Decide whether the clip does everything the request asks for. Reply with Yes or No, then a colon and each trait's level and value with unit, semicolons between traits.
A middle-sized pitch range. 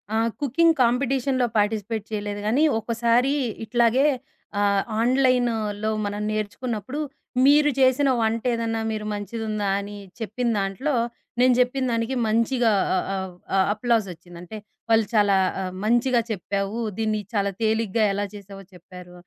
Yes: average, 3.3 semitones